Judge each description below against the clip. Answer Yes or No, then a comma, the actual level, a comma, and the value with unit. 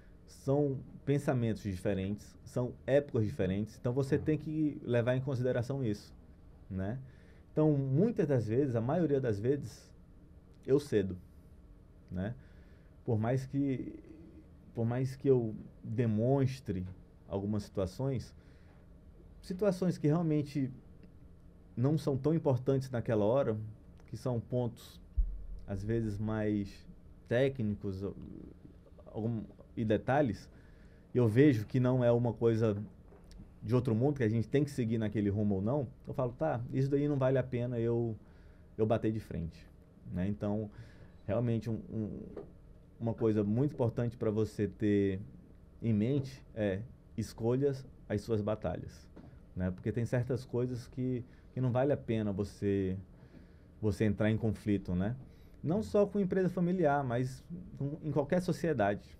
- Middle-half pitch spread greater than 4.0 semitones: Yes, wide, 5.5 semitones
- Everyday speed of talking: Yes, average, 140 wpm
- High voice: No, low, 115 Hz